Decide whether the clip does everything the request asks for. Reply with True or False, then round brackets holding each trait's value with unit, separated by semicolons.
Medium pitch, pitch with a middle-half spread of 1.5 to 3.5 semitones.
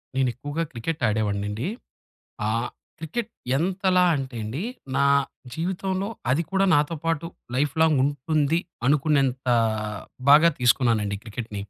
False (145 Hz; 5.5 semitones)